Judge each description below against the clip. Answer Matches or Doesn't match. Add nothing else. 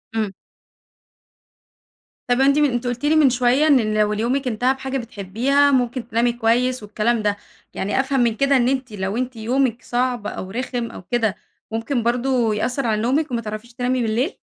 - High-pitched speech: Matches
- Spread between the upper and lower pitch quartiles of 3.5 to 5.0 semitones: Doesn't match